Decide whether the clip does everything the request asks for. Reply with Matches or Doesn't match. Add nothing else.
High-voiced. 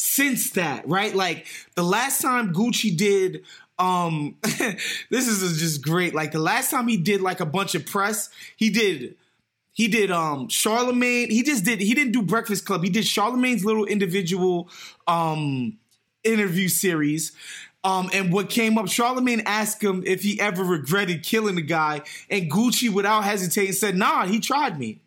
Matches